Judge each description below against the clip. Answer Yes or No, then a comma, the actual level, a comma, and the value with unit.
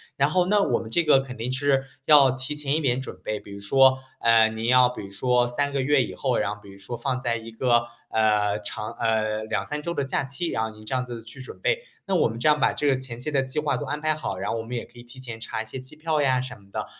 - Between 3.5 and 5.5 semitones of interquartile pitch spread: Yes, average, 3.8 semitones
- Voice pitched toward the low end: Yes, low, 125 Hz